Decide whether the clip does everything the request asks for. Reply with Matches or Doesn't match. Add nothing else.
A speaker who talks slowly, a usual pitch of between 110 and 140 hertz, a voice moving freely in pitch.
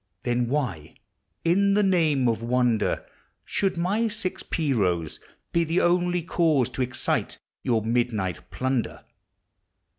Matches